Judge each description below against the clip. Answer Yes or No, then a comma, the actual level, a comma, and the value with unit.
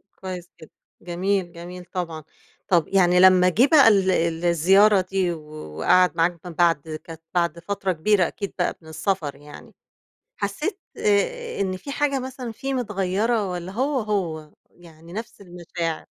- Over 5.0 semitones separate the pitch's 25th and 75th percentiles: No, average, 3.3 semitones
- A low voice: No, medium, 185 Hz